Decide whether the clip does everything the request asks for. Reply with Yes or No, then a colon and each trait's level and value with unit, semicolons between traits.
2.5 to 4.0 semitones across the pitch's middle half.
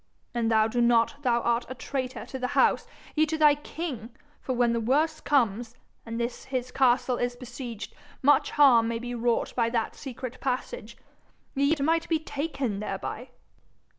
Yes: average, 3.2 semitones